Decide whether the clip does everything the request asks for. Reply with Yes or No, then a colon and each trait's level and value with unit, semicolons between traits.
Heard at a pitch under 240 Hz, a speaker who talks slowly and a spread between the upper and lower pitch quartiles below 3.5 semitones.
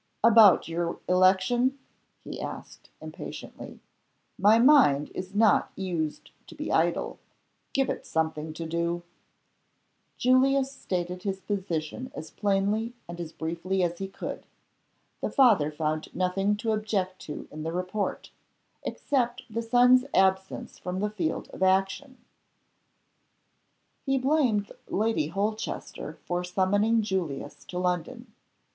No: high, 190 Hz; slow, 125 wpm; average, 4.7 semitones